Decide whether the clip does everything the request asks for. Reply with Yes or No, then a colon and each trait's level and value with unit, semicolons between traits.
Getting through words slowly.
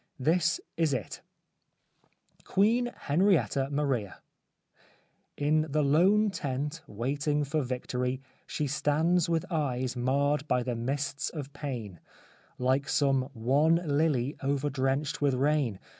Yes: slow, 115 wpm